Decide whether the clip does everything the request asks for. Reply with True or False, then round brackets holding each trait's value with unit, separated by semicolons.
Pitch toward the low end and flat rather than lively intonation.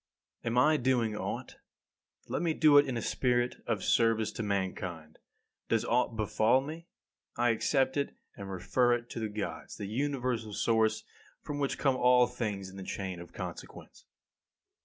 False (120 Hz; 3.9 semitones)